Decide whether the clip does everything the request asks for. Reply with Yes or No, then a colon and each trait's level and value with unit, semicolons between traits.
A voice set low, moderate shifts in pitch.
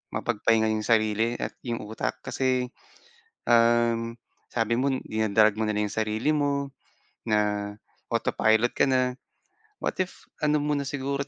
Yes: low, 115 Hz; average, 3.6 semitones